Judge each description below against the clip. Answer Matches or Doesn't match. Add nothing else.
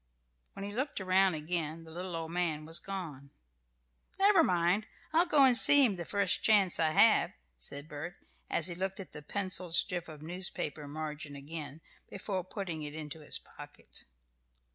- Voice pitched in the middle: Matches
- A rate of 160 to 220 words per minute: Matches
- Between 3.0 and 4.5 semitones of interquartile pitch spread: Matches